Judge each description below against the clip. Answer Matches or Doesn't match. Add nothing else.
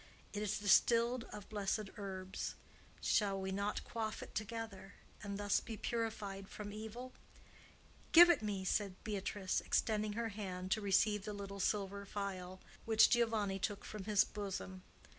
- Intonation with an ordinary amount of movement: Doesn't match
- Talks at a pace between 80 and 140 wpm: Doesn't match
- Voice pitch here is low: Doesn't match